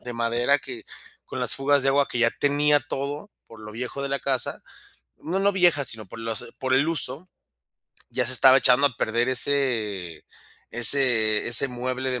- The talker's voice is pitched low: Yes, low, 130 Hz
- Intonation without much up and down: No, average, 3.2 semitones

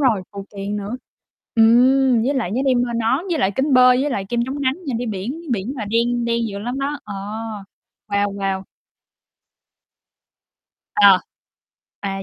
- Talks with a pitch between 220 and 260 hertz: Yes, high, 235 Hz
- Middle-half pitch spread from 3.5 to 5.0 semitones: Yes, average, 4.4 semitones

